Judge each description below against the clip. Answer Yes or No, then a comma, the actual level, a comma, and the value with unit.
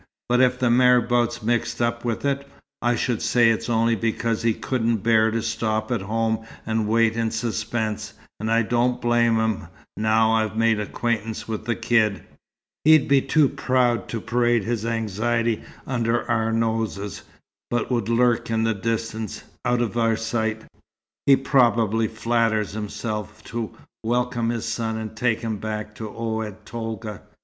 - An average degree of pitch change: No, narrow, 1.4 semitones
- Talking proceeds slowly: No, average, 160 wpm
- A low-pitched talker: Yes, low, 115 Hz